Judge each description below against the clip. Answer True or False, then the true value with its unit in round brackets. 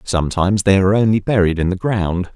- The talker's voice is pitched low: True (95 Hz)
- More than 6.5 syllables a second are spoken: False (6.2 syllables/s)